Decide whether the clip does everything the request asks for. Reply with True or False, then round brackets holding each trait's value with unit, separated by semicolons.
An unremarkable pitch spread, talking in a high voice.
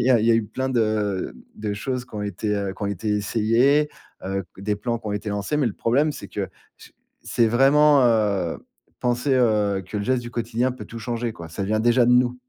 False (3.3 semitones; 115 Hz)